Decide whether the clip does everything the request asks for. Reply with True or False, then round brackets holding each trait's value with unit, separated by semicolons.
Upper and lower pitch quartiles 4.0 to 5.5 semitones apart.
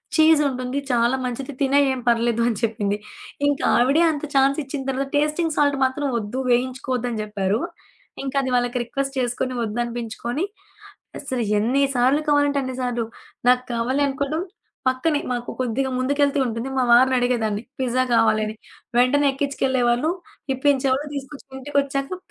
False (2.7 semitones)